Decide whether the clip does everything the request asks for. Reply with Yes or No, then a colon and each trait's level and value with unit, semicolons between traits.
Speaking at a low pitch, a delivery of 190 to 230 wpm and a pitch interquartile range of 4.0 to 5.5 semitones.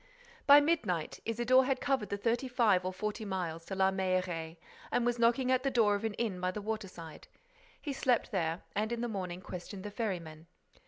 No: high, 205 Hz; average, 200 wpm; average, 4.7 semitones